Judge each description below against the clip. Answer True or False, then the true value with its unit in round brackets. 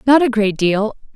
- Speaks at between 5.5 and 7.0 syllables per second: False (4.7 syllables/s)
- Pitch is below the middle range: False (225 Hz)